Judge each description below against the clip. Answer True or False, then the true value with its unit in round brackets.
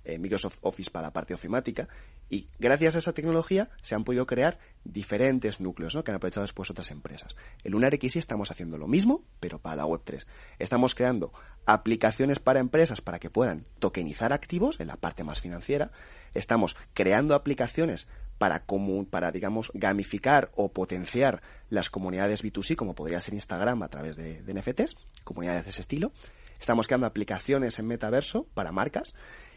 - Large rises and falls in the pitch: True (5.7 semitones)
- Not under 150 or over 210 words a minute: True (170 wpm)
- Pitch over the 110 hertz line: False (105 Hz)